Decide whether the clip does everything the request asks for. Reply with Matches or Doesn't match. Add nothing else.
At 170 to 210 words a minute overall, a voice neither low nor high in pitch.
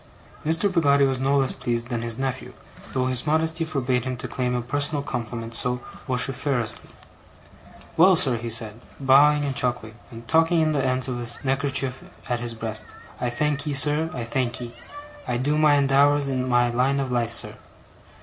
Doesn't match